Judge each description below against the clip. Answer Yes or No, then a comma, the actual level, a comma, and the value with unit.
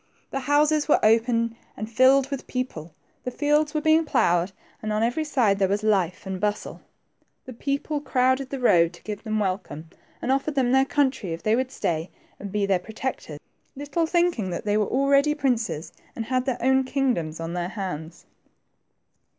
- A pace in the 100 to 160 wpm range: No, average, 180 wpm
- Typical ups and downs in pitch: No, wide, 6.0 semitones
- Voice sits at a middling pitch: No, high, 235 Hz